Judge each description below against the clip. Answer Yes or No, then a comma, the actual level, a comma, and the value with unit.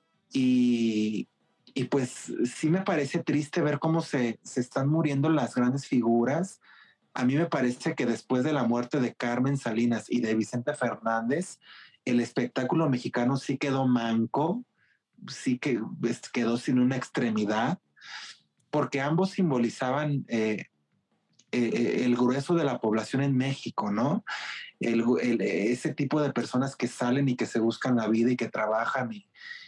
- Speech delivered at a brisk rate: No, average, 155 wpm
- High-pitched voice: No, low, 125 Hz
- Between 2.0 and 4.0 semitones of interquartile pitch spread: Yes, average, 3.7 semitones